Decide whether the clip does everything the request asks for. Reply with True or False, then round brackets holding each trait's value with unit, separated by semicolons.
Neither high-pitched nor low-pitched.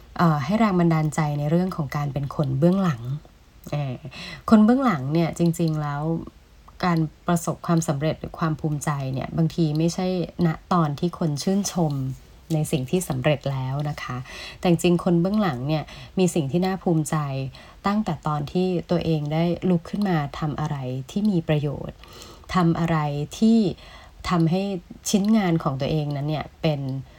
True (165 Hz)